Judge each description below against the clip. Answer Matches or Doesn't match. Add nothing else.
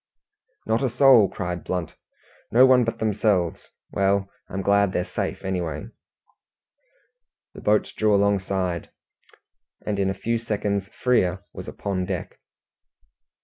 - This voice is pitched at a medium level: Doesn't match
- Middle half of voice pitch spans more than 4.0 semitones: Doesn't match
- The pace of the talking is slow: Matches